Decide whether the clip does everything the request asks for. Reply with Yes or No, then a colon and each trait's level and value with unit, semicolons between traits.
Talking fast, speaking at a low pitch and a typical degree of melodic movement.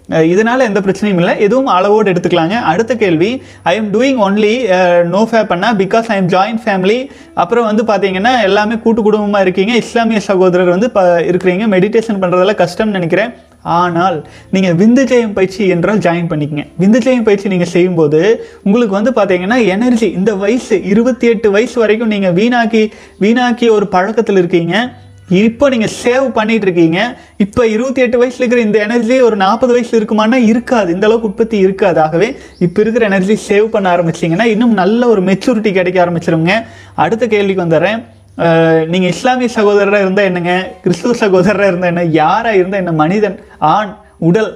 No: fast, 155 wpm; high, 205 Hz; average, 3.9 semitones